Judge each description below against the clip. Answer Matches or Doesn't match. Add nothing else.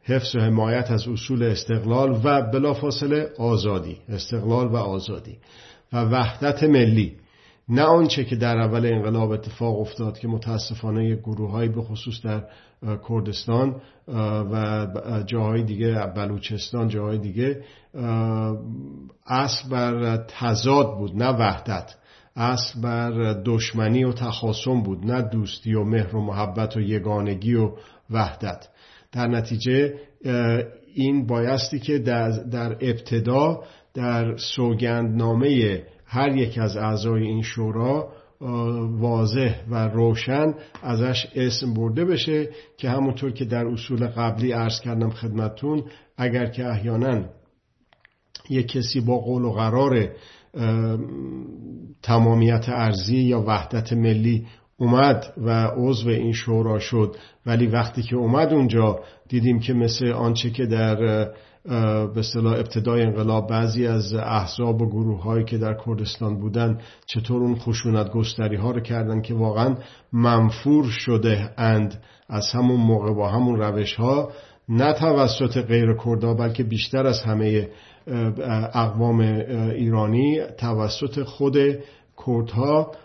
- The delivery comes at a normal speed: Matches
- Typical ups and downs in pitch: Doesn't match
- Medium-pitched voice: Doesn't match